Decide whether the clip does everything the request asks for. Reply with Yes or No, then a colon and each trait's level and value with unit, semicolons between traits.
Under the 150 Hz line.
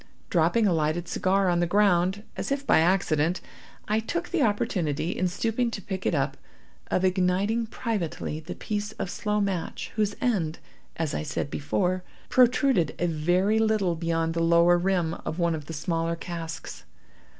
No: medium, 180 Hz